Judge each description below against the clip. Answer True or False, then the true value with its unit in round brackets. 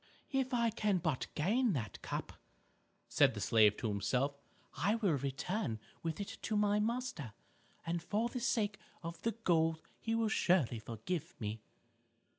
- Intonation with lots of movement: True (8.7 semitones)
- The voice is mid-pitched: True (180 Hz)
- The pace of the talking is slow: False (155 wpm)